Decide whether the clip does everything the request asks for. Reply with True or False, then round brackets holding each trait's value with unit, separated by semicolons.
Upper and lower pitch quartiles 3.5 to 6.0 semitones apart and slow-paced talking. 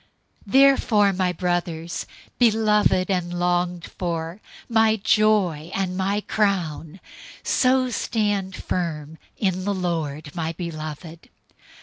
True (3.8 semitones; 100 wpm)